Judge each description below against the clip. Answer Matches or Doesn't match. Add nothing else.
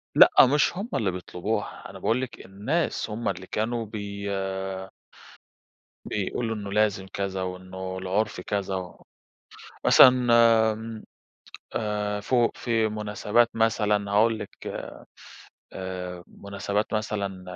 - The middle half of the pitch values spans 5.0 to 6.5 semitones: Doesn't match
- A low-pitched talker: Matches